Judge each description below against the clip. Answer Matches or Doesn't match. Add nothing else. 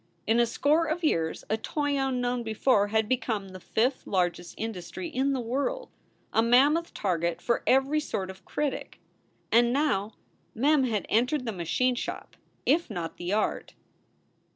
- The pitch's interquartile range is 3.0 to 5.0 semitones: Doesn't match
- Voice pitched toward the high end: Matches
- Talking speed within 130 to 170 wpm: Matches